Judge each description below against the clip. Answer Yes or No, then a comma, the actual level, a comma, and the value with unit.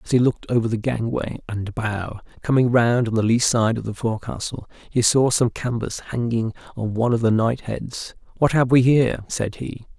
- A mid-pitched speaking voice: No, low, 115 Hz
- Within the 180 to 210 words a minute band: Yes, average, 200 wpm